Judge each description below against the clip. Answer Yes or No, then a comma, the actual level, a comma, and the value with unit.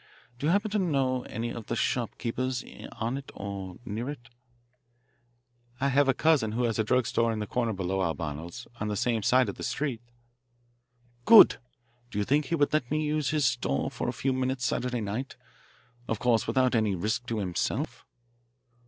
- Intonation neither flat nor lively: Yes, average, 4.1 semitones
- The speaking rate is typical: Yes, average, 190 wpm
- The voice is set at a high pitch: No, low, 120 Hz